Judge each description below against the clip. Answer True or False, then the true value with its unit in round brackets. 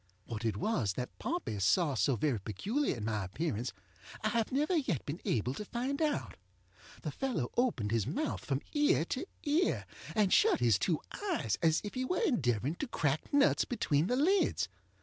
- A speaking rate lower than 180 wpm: False (185 wpm)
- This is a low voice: False (170 Hz)